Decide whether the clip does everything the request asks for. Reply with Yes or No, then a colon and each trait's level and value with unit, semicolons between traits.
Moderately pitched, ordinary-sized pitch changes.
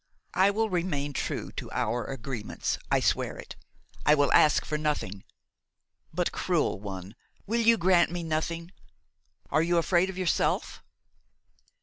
Yes: medium, 165 Hz; average, 4.3 semitones